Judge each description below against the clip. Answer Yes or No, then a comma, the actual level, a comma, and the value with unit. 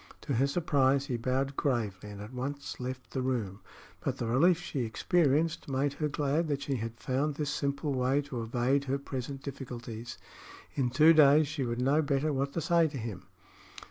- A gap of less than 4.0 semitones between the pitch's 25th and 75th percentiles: Yes, average, 2.7 semitones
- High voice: No, low, 135 Hz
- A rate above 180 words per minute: Yes, average, 190 wpm